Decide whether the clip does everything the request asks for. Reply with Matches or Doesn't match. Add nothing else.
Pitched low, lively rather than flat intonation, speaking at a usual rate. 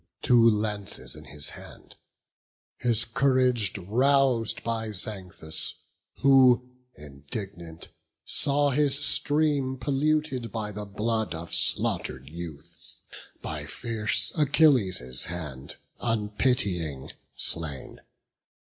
Doesn't match